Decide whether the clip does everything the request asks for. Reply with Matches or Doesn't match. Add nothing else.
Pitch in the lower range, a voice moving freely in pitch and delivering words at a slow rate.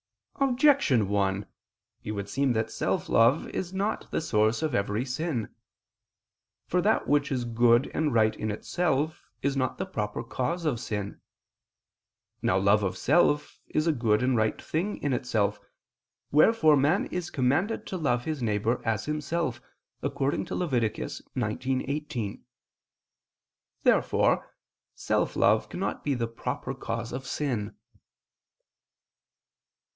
Matches